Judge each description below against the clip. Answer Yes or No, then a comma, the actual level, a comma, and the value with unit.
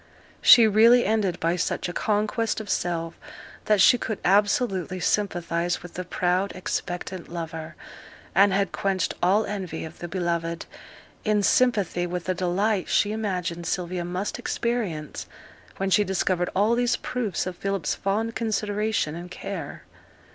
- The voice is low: No, high, 190 Hz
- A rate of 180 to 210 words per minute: No, average, 145 wpm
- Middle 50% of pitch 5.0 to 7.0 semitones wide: No, average, 3.1 semitones